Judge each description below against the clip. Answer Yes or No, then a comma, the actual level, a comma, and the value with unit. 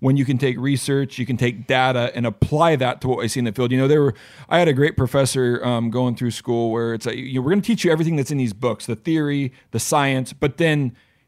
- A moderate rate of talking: No, fast, 275 wpm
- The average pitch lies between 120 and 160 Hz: Yes, low, 130 Hz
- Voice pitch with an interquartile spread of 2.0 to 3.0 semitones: Yes, average, 2.7 semitones